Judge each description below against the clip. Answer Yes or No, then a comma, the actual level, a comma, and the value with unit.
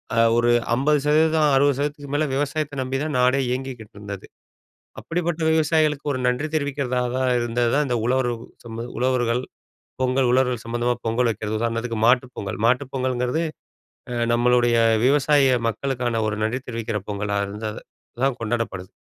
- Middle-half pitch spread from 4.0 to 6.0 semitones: No, average, 3.3 semitones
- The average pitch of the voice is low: Yes, low, 125 Hz